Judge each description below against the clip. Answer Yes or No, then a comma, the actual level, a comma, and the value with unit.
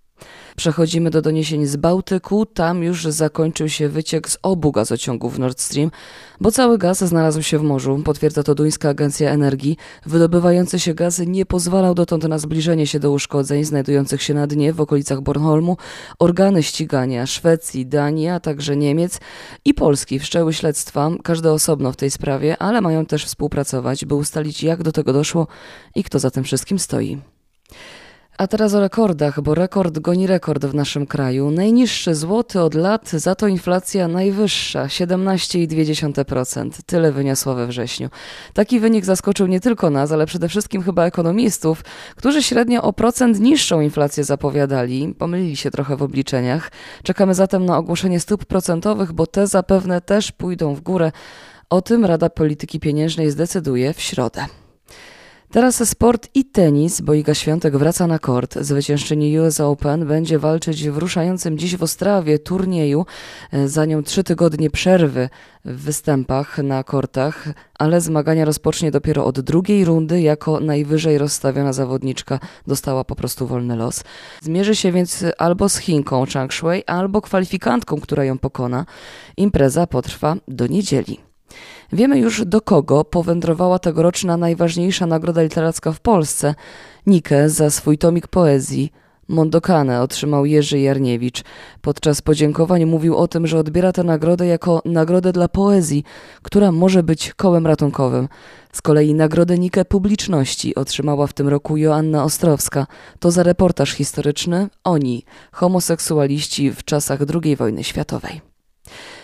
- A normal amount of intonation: Yes, average, 3.7 semitones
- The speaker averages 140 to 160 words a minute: Yes, average, 145 wpm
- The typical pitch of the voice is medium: Yes, medium, 160 Hz